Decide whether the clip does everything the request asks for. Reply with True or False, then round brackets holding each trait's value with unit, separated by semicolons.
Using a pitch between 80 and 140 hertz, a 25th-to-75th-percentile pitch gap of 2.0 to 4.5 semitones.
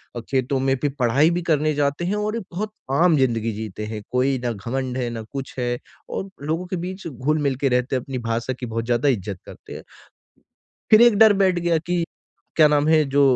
False (135 Hz; 5.2 semitones)